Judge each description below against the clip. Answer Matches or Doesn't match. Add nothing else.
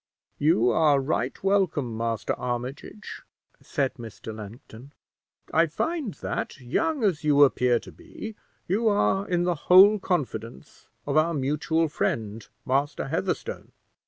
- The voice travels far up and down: Matches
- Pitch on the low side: Doesn't match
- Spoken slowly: Matches